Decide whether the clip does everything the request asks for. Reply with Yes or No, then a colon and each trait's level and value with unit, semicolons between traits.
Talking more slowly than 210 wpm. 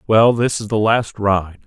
No: fast, 215 wpm